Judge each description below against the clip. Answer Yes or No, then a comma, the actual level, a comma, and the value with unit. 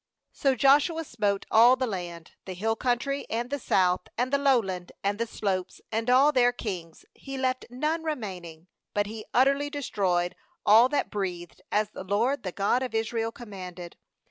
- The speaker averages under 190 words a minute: Yes, average, 170 wpm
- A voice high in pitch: Yes, high, 225 Hz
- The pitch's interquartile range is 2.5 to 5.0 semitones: No, wide, 5.4 semitones